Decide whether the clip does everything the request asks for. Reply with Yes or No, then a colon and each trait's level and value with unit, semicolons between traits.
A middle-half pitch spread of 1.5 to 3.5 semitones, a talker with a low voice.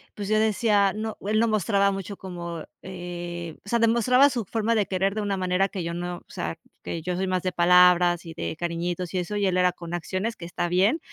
No: average, 3.1 semitones; medium, 185 Hz